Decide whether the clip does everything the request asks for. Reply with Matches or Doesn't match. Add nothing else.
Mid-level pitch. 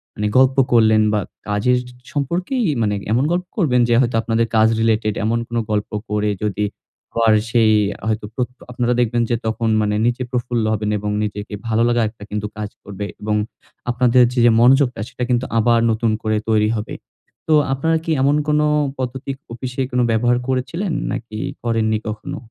Doesn't match